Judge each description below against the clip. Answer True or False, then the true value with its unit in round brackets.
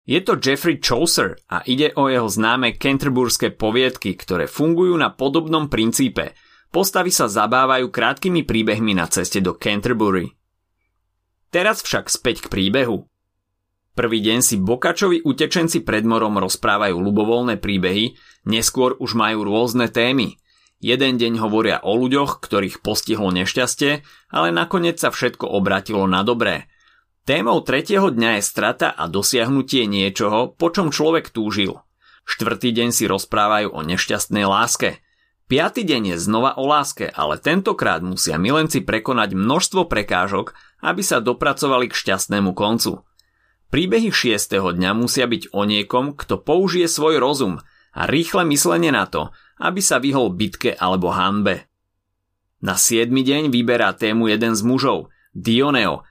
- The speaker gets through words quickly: False (140 wpm)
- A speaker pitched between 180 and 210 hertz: False (115 Hz)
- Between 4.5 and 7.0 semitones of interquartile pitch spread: True (5.4 semitones)